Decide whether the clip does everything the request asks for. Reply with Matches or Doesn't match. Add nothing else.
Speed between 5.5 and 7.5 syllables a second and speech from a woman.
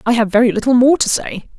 Matches